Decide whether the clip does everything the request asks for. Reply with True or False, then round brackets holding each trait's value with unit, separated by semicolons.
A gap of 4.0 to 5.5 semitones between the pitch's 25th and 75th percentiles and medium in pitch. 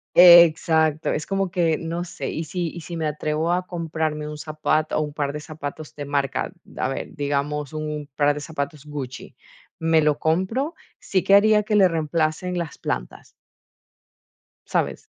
False (2.6 semitones; 155 Hz)